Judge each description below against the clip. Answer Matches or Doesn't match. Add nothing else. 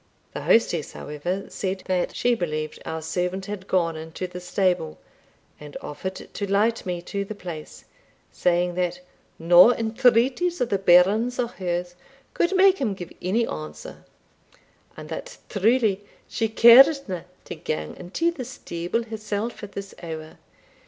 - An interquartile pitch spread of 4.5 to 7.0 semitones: Matches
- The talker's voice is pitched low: Doesn't match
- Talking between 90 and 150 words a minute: Matches